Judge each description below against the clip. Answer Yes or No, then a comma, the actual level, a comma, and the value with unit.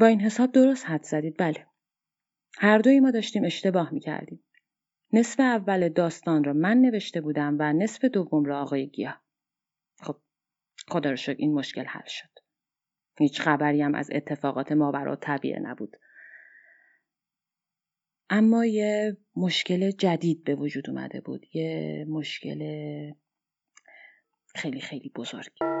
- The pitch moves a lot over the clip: Yes, wide, 6.3 semitones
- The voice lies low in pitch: No, medium, 165 Hz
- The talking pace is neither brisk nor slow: Yes, average, 130 wpm